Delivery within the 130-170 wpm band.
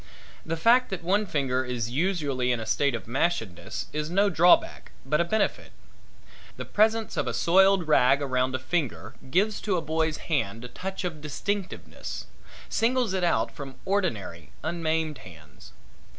Yes: average, 160 wpm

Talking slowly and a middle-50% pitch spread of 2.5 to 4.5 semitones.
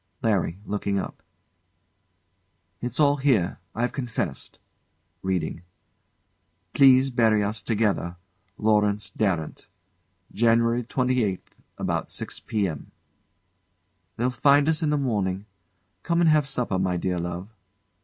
No: slow, 115 wpm; average, 5.1 semitones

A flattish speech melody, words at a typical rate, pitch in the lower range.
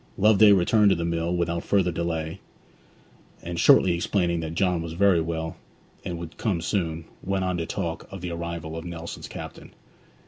Yes: narrow, 2.0 semitones; average, 175 wpm; very low, 85 Hz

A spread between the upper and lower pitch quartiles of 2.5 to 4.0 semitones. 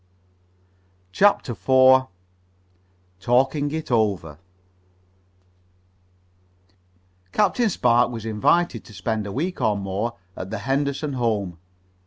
No: average, 5.1 semitones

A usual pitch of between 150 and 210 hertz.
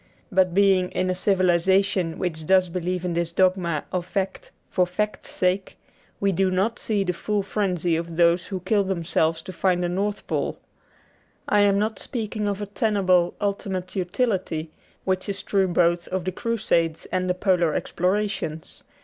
Yes: medium, 185 Hz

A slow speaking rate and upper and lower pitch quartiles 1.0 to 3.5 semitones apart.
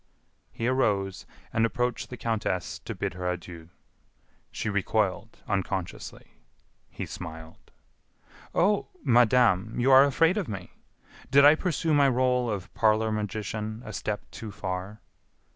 No: slow, 130 wpm; average, 4.5 semitones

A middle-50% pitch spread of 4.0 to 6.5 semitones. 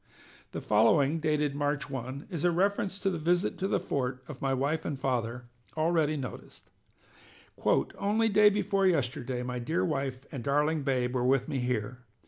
Yes: average, 4.9 semitones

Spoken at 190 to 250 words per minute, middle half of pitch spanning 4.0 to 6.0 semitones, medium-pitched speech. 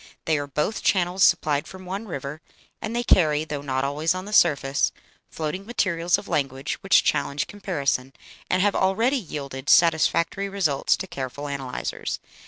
No: average, 160 wpm; average, 5.2 semitones; medium, 160 Hz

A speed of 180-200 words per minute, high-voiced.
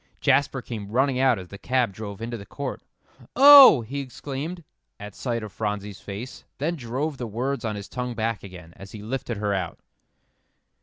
No: average, 185 wpm; low, 120 Hz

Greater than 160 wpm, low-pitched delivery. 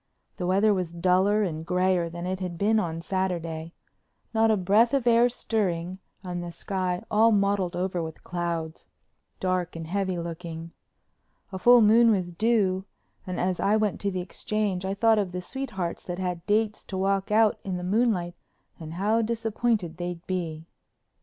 No: average, 170 wpm; medium, 185 Hz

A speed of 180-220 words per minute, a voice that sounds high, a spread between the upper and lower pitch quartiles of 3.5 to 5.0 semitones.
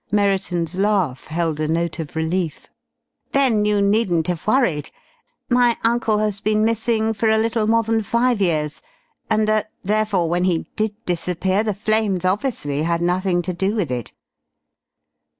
No: average, 155 wpm; high, 200 Hz; average, 4.2 semitones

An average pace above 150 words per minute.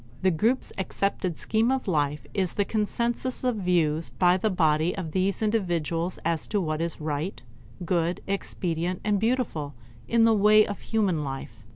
Yes: average, 170 wpm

